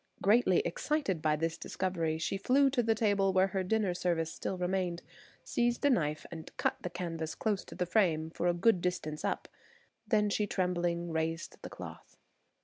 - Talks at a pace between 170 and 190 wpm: Yes, average, 180 wpm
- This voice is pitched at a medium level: Yes, medium, 180 Hz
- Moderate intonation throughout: Yes, average, 3.8 semitones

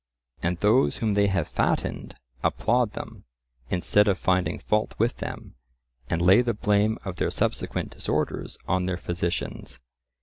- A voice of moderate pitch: No, low, 100 Hz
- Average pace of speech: Yes, average, 145 wpm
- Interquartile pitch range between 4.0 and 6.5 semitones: No, average, 3.0 semitones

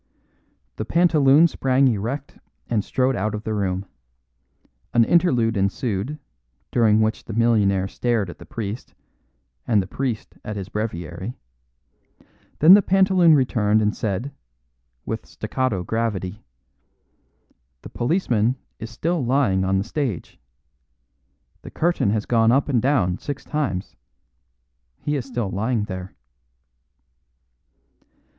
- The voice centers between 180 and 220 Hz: No, low, 115 Hz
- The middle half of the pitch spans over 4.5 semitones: Yes, average, 5.0 semitones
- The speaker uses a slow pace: Yes, slow, 125 wpm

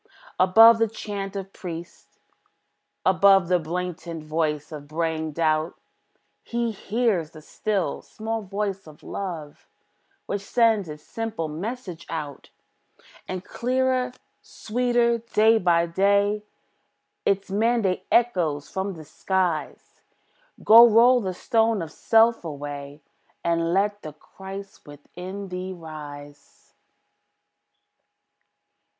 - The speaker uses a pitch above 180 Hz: Yes, high, 190 Hz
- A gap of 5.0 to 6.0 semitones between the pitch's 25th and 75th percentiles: Yes, average, 5.3 semitones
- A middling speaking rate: No, slow, 110 wpm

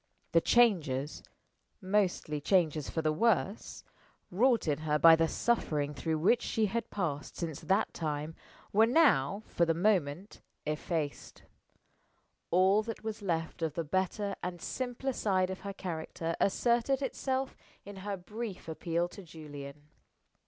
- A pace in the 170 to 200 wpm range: No, average, 140 wpm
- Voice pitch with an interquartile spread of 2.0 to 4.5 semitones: No, average, 5.2 semitones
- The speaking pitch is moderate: Yes, medium, 180 Hz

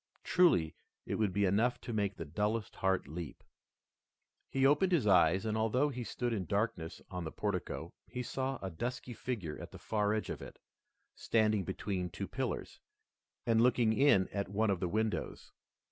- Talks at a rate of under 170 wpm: No, average, 175 wpm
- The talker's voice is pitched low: Yes, low, 105 Hz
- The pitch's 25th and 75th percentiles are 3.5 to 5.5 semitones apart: Yes, average, 4.2 semitones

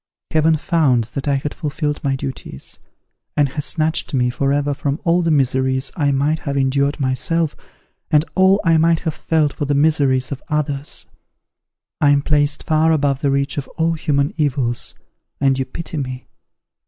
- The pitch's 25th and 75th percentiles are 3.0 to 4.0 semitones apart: No, narrow, 2.5 semitones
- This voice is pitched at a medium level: Yes, medium, 145 Hz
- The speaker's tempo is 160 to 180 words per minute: Yes, average, 175 wpm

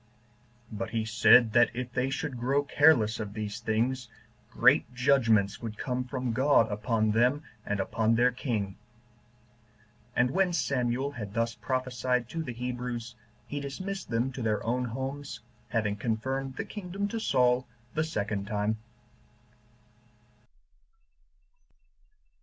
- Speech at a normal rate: No, slow, 130 wpm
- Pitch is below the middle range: Yes, low, 125 Hz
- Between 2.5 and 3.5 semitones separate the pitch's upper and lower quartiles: Yes, average, 3.2 semitones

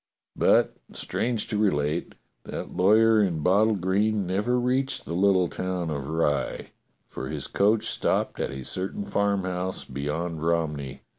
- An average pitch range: Yes, average, 4.6 semitones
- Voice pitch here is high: No, very low, 95 Hz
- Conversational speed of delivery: Yes, average, 145 wpm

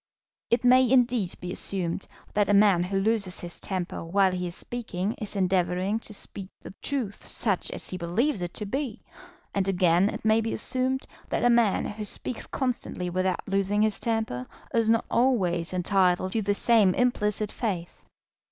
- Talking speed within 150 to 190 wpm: Yes, average, 175 wpm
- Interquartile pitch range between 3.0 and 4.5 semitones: Yes, average, 3.8 semitones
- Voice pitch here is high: Yes, high, 200 Hz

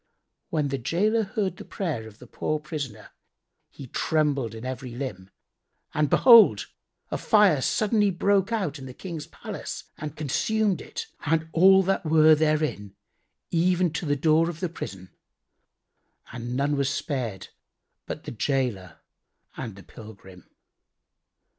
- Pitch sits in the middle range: Yes, medium, 150 Hz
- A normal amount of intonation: No, wide, 6.1 semitones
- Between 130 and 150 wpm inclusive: Yes, average, 140 wpm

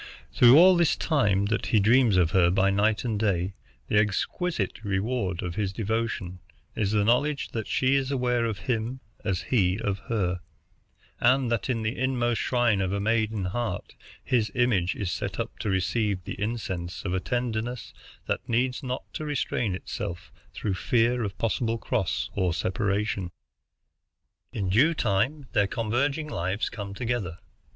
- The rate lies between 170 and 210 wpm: No, average, 160 wpm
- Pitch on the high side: No, low, 110 Hz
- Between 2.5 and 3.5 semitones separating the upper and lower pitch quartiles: No, average, 4.0 semitones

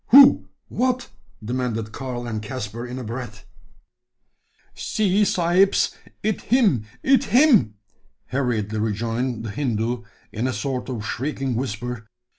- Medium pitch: No, low, 125 Hz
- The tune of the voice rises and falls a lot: Yes, wide, 7.1 semitones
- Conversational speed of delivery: No, slow, 120 wpm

